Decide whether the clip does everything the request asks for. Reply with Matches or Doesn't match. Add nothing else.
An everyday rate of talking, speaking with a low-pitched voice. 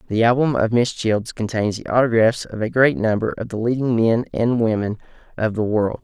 Doesn't match